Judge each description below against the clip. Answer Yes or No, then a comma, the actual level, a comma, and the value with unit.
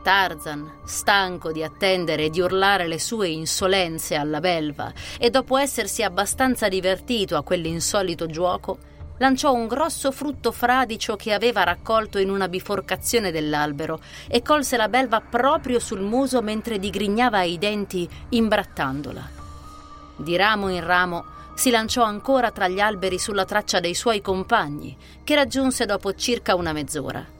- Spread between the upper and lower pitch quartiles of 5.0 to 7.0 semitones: Yes, wide, 5.4 semitones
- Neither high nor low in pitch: No, high, 195 Hz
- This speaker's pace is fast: No, average, 140 wpm